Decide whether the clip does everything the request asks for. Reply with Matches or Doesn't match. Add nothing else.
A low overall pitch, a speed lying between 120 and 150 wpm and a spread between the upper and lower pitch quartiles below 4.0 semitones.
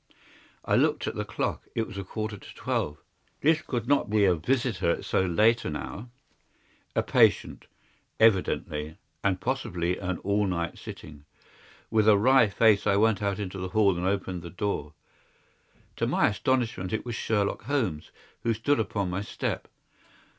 Doesn't match